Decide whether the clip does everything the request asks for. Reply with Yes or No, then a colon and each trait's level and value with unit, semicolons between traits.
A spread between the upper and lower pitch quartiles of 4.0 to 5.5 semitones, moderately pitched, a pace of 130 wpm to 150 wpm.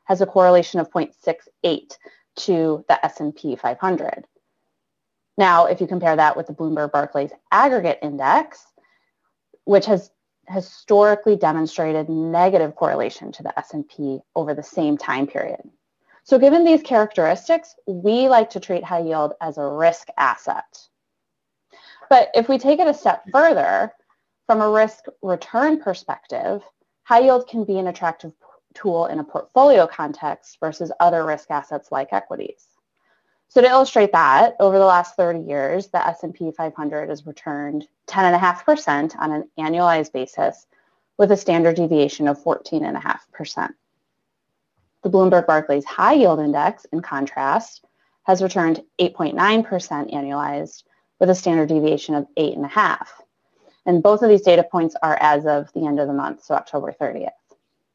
Yes: average, 5.2 semitones; medium, 170 Hz; average, 140 wpm